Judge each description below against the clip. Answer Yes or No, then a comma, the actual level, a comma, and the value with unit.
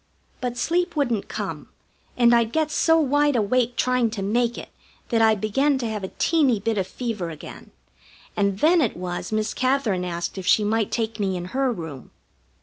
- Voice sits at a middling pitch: No, high, 230 Hz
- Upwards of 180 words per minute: Yes, average, 190 wpm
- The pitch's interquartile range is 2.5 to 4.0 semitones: No, average, 4.6 semitones